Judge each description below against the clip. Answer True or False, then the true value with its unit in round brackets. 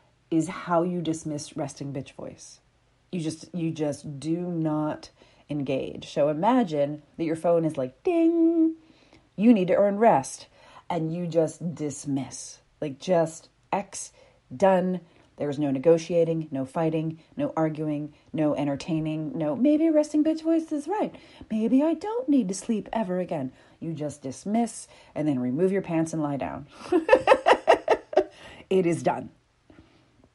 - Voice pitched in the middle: True (165 Hz)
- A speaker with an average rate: True (145 wpm)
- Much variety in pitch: True (6.7 semitones)